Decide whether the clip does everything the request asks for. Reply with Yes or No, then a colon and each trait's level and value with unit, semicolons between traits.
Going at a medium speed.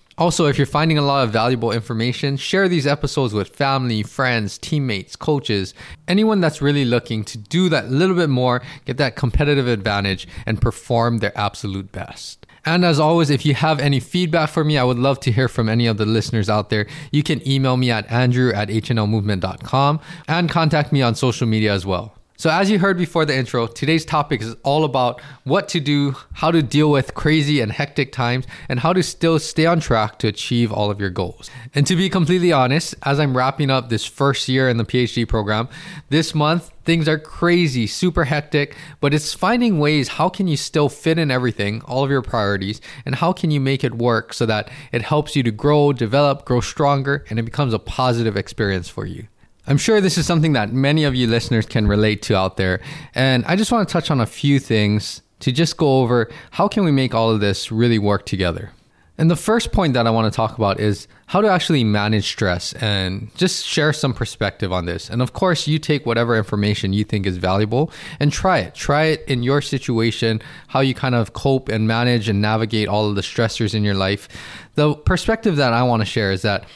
No: fast, 220 wpm